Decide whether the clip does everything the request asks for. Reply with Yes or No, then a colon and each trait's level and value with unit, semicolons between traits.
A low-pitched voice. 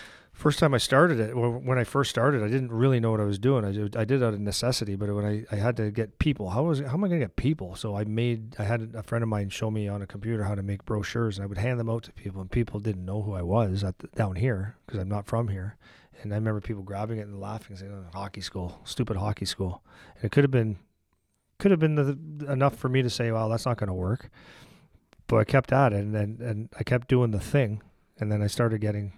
Yes: low, 110 Hz